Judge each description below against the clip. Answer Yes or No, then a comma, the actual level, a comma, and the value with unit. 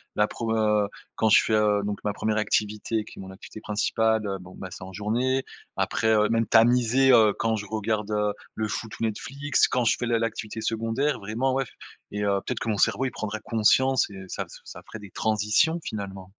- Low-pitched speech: Yes, low, 110 Hz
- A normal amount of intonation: No, narrow, 1.7 semitones